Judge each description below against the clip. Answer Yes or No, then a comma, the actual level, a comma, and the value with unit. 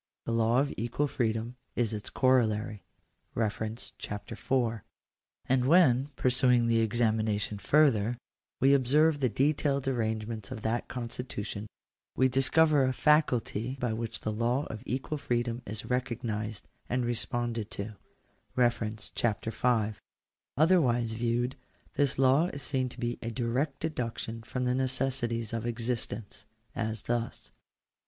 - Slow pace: Yes, slow, 130 wpm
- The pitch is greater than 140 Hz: No, low, 120 Hz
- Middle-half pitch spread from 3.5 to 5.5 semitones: No, average, 2.7 semitones